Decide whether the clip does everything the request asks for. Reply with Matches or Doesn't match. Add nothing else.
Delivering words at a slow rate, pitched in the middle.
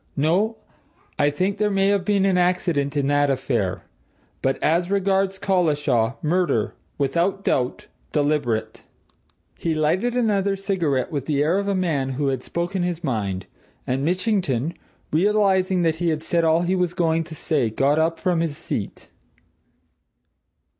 Doesn't match